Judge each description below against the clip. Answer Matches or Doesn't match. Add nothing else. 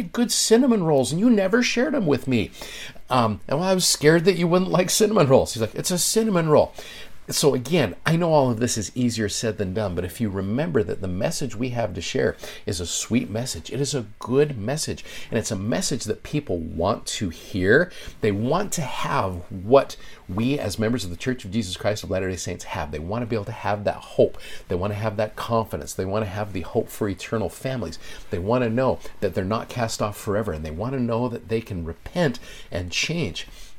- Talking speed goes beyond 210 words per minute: Matches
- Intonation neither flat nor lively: Doesn't match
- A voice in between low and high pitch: Doesn't match